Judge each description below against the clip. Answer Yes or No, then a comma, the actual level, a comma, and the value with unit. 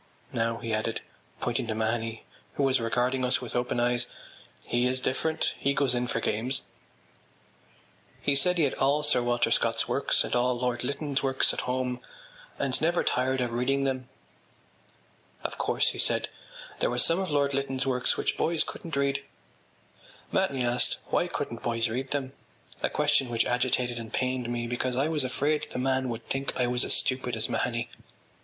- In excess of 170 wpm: Yes, average, 180 wpm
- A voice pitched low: Yes, low, 125 Hz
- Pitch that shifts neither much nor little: No, narrow, 2.2 semitones